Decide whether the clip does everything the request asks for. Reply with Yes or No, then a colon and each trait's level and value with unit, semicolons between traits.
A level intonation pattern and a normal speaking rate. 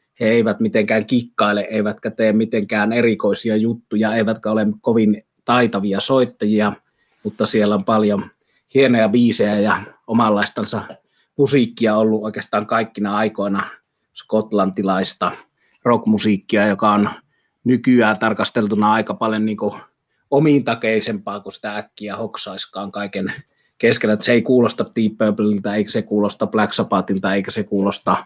Yes: narrow, 1.7 semitones; average, 120 wpm